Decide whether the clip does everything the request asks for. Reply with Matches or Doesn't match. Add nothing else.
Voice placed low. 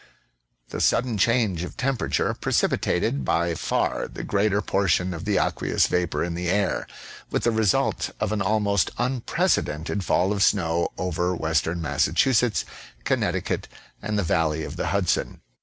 Matches